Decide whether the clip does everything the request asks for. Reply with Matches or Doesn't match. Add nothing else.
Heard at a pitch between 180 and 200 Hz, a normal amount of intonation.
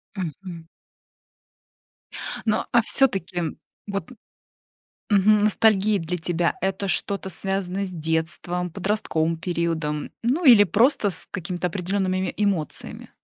Matches